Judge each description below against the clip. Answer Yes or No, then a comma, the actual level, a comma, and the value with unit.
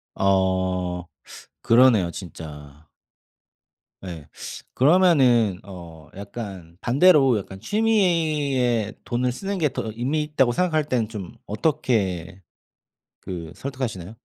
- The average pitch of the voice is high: No, low, 115 Hz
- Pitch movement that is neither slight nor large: No, wide, 7.3 semitones